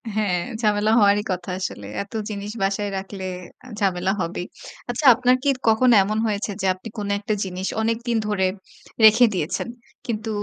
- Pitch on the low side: No, high, 205 Hz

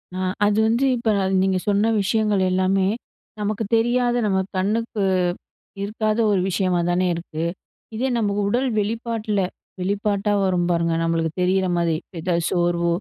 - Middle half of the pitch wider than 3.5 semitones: No, average, 3.2 semitones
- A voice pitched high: Yes, high, 200 Hz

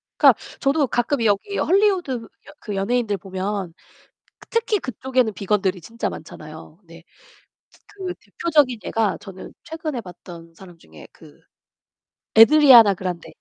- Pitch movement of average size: No, wide, 7.0 semitones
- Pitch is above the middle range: Yes, high, 220 Hz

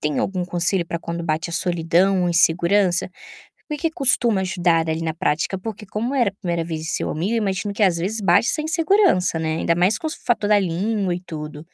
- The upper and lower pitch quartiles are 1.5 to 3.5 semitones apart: No, average, 3.9 semitones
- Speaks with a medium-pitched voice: Yes, medium, 180 Hz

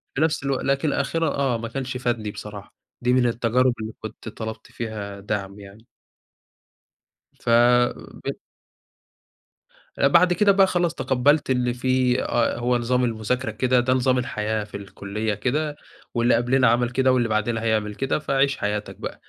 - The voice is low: Yes, low, 120 Hz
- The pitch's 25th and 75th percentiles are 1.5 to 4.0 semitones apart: Yes, average, 3.2 semitones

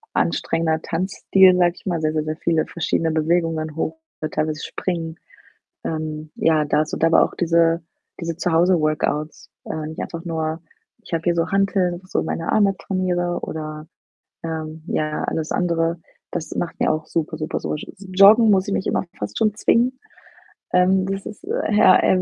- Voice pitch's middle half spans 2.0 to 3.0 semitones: Yes, average, 2.7 semitones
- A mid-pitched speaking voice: Yes, medium, 165 Hz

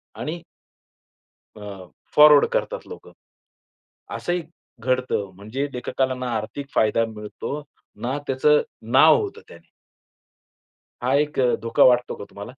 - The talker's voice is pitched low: Yes, low, 130 Hz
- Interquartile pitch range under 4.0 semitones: No, average, 4.4 semitones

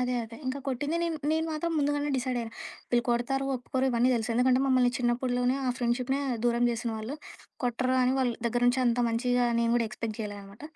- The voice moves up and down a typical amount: No, narrow, 1.8 semitones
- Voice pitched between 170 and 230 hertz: No, high, 245 Hz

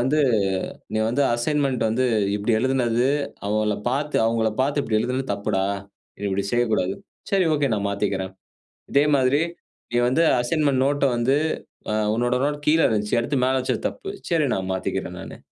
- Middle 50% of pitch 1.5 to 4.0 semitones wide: No, average, 4.5 semitones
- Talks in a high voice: No, low, 125 Hz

